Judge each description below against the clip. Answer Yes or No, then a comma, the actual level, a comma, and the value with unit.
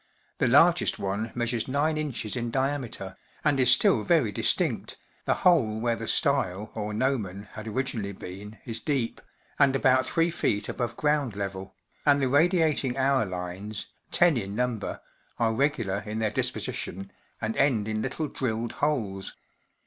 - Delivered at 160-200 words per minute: No, average, 150 wpm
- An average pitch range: Yes, average, 5.0 semitones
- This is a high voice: No, low, 120 Hz